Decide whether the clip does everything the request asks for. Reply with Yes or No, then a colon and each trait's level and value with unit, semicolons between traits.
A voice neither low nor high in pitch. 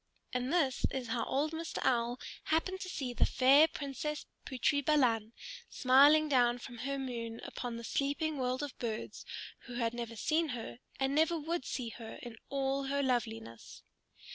No: very high, 260 Hz